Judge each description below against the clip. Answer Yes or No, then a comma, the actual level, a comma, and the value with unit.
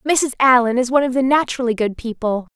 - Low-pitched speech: No, very high, 250 Hz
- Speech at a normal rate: No, fast, 210 wpm